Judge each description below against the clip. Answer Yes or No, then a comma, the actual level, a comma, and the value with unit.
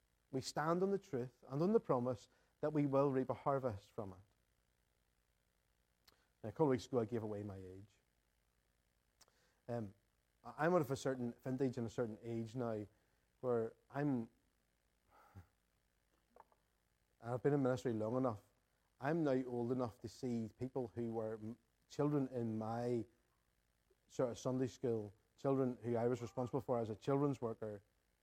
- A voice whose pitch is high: No, low, 115 Hz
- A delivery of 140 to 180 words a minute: Yes, average, 160 wpm